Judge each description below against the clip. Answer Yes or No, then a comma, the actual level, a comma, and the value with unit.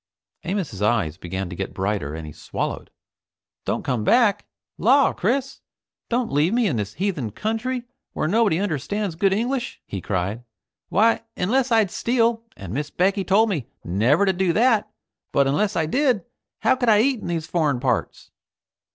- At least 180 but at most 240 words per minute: No, average, 170 wpm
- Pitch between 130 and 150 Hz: No, high, 190 Hz